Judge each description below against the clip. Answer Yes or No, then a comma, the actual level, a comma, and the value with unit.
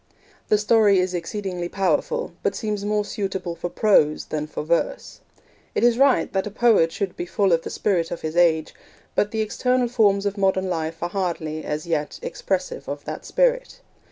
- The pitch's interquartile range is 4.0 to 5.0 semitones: Yes, average, 4.3 semitones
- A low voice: No, high, 195 Hz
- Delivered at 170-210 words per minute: Yes, average, 185 wpm